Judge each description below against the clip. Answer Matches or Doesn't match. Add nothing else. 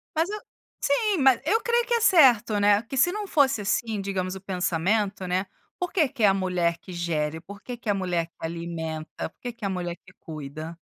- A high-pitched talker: Matches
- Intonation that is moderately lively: Doesn't match